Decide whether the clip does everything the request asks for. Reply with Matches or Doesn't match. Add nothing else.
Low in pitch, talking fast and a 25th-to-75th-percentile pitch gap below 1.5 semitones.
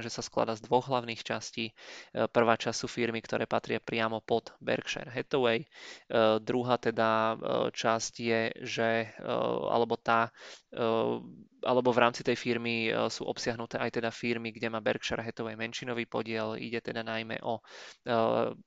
Doesn't match